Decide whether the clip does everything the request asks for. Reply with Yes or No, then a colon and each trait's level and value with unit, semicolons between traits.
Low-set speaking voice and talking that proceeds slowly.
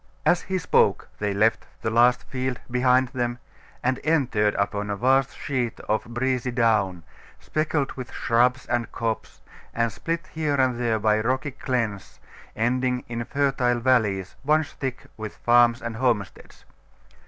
No: low, 120 Hz; average, 145 wpm